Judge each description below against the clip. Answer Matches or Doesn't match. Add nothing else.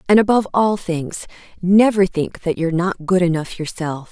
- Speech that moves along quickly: Doesn't match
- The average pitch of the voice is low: Doesn't match